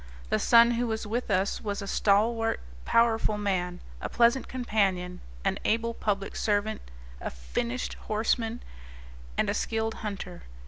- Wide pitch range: No, narrow, 2.6 semitones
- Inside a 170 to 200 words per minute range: No, average, 140 wpm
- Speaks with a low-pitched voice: No, high, 220 Hz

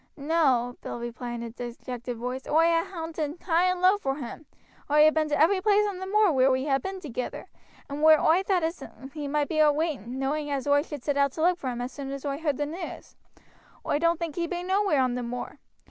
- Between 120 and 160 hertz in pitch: No, very high, 295 Hz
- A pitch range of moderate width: Yes, average, 4.2 semitones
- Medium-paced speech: No, fast, 245 wpm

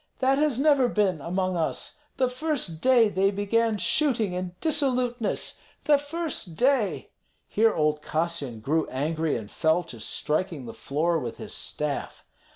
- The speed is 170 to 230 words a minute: No, average, 150 wpm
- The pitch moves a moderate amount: No, wide, 8.1 semitones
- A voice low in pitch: No, high, 190 Hz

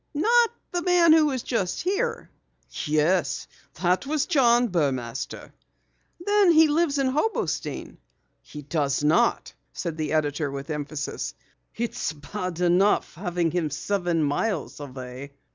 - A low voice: No, medium, 180 Hz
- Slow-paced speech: Yes, slow, 125 wpm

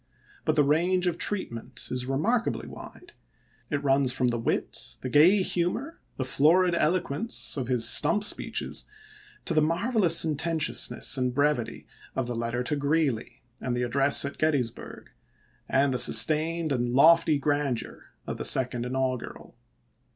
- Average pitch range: Yes, average, 4.7 semitones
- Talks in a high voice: No, medium, 145 Hz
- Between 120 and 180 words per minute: Yes, average, 145 wpm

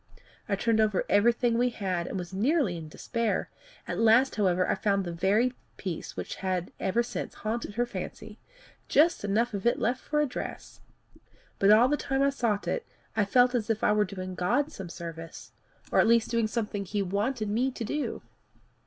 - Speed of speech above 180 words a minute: Yes, average, 190 wpm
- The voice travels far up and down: No, average, 3.8 semitones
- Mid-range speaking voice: No, high, 215 Hz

